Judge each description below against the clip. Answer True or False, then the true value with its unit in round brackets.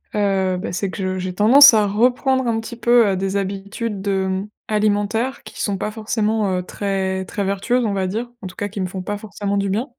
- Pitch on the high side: True (205 Hz)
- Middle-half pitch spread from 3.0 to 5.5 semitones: False (2.5 semitones)